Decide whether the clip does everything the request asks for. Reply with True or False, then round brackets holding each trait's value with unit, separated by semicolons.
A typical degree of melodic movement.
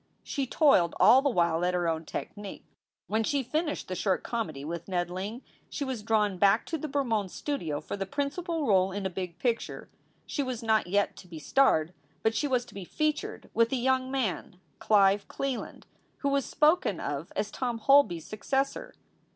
False (6.8 semitones)